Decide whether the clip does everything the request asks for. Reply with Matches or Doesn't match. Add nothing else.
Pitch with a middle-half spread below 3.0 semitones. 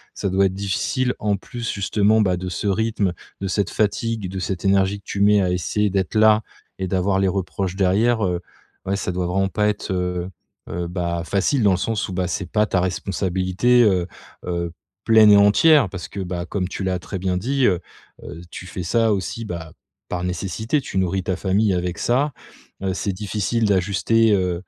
Matches